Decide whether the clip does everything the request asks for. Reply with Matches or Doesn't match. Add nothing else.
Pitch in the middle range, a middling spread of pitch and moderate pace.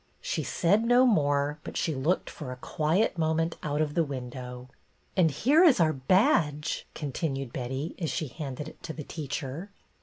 Matches